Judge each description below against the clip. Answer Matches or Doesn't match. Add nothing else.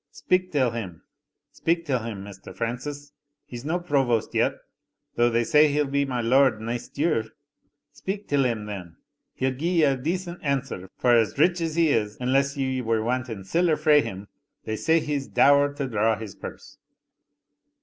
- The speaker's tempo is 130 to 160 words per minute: Doesn't match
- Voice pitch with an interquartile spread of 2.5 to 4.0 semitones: Doesn't match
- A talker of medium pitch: Doesn't match